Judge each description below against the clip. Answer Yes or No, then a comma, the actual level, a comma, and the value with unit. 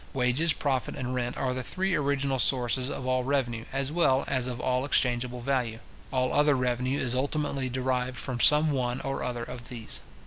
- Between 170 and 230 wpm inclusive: Yes, average, 185 wpm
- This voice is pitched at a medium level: No, low, 130 Hz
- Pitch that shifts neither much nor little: No, narrow, 1.7 semitones